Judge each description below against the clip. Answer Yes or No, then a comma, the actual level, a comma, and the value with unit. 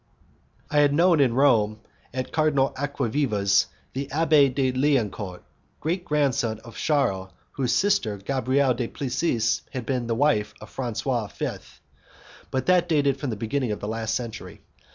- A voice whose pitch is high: No, low, 130 Hz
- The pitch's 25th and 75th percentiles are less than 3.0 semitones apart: No, average, 4.2 semitones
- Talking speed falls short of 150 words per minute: No, average, 155 wpm